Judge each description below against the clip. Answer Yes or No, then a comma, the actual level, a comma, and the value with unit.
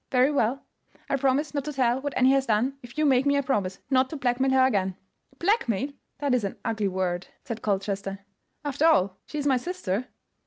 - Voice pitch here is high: Yes, very high, 255 Hz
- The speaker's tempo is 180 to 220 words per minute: Yes, fast, 205 wpm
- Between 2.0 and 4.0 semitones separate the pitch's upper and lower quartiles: No, average, 5.0 semitones